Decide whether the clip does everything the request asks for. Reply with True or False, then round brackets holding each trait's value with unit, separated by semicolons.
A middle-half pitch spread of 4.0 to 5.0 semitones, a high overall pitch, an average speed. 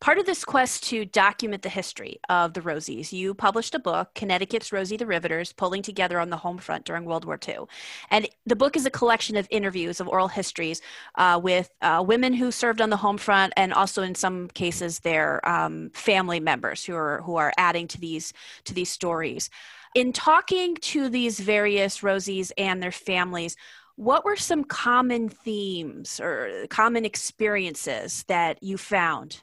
True (4.5 semitones; 195 Hz; 180 wpm)